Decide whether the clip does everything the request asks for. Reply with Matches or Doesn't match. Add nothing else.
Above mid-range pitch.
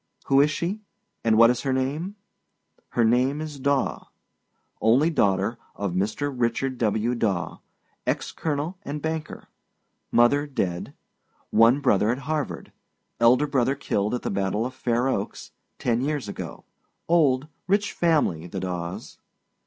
Doesn't match